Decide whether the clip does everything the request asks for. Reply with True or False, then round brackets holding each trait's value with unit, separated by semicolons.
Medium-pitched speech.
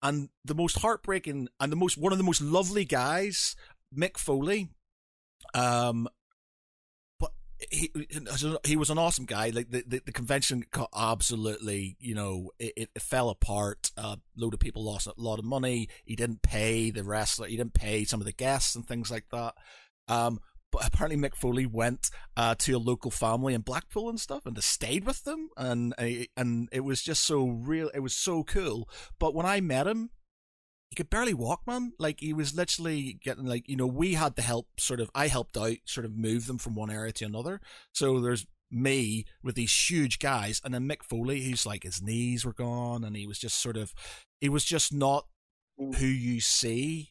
False (125 Hz)